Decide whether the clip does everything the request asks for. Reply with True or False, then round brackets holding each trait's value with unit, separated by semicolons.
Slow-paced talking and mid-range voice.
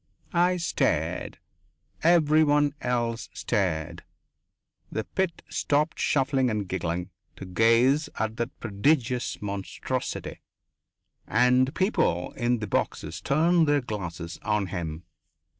False (105 wpm; 120 Hz)